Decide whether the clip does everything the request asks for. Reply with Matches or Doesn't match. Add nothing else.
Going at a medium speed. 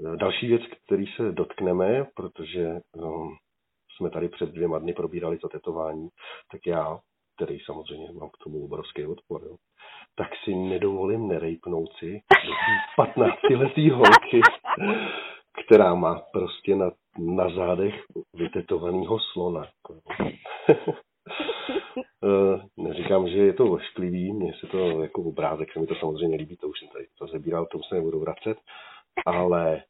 Matches